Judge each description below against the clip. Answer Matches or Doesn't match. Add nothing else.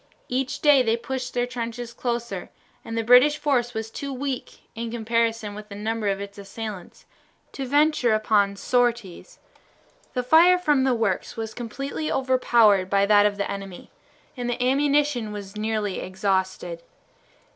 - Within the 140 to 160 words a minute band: Matches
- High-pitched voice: Matches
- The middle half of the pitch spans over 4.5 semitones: Doesn't match